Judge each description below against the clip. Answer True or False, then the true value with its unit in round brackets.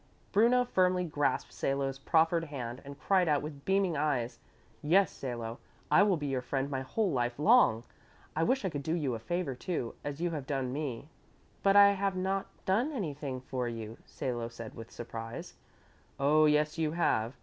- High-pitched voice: False (145 Hz)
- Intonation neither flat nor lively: False (6.0 semitones)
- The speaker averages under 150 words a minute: False (185 wpm)